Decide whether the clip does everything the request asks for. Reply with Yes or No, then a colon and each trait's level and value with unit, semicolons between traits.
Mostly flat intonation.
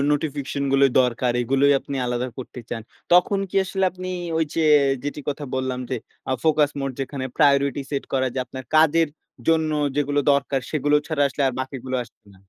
Yes: narrow, 2.3 semitones